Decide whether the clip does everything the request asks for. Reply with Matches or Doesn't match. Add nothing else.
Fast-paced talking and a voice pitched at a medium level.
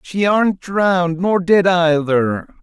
Doesn't match